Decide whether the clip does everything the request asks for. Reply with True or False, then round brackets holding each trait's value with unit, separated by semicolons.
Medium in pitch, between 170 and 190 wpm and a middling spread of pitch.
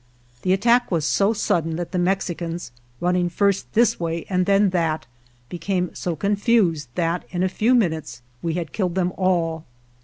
True (180 Hz; 175 wpm; 3.0 semitones)